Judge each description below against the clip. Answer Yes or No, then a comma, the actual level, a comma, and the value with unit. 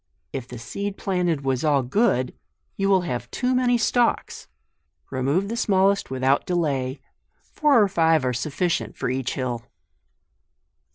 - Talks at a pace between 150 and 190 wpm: No, average, 140 wpm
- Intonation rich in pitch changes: Yes, wide, 7.4 semitones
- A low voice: No, medium, 160 Hz